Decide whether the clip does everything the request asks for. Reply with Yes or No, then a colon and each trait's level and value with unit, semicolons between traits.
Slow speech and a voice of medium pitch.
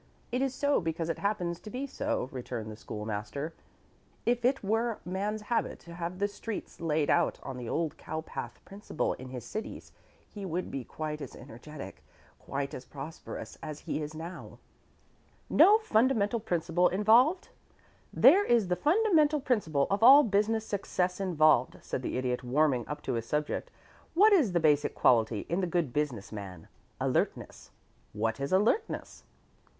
No: average, 165 wpm; medium, 170 Hz